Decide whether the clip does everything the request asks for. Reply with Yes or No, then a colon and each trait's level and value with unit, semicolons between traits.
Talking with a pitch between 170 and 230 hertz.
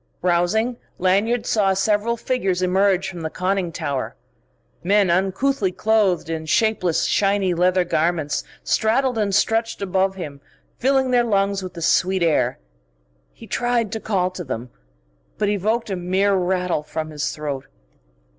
Yes: high, 190 Hz